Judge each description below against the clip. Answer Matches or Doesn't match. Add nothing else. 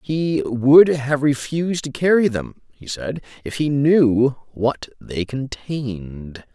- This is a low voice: Matches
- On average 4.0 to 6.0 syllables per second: Doesn't match